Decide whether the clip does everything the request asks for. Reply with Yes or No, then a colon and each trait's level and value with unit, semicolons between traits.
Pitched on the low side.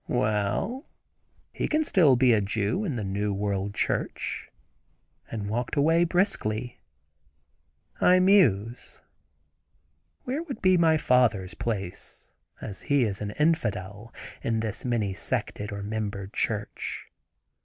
Yes: low, 110 Hz